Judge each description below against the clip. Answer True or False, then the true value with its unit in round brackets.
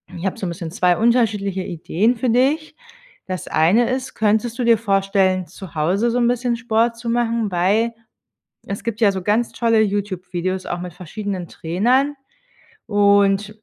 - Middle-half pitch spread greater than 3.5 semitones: True (3.9 semitones)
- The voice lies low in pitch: False (205 Hz)